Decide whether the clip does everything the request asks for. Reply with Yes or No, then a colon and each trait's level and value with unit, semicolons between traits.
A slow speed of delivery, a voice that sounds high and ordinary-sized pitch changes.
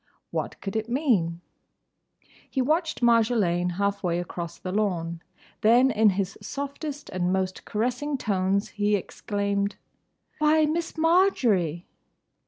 No: slow, 120 wpm; high, 210 Hz; wide, 6.4 semitones